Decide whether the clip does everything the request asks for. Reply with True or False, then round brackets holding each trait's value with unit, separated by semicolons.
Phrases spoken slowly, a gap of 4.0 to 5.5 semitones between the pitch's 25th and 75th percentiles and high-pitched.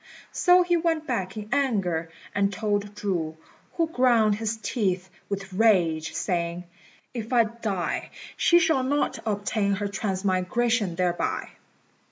True (130 wpm; 4.4 semitones; 205 Hz)